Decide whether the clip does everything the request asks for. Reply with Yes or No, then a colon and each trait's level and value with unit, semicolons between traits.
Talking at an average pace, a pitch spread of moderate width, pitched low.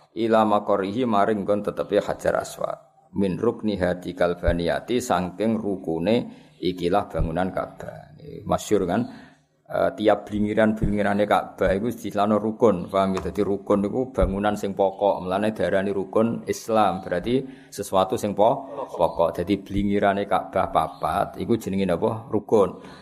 No: average, 130 wpm; narrow, 1.9 semitones; low, 100 Hz